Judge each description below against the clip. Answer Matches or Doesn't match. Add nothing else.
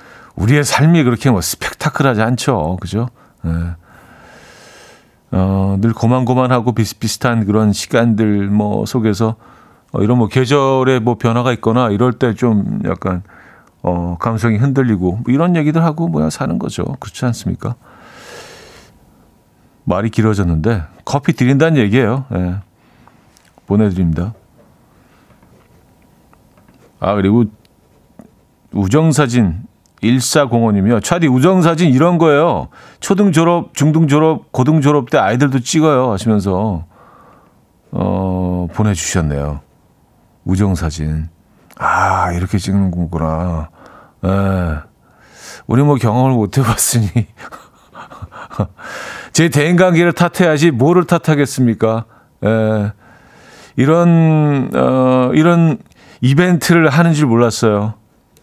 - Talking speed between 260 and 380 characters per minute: Doesn't match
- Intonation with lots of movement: Matches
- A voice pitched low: Matches